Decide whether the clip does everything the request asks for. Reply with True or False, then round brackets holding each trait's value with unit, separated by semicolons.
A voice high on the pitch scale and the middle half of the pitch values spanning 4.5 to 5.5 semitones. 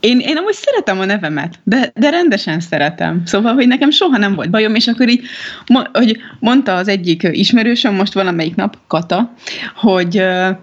True (215 Hz; 5.1 semitones)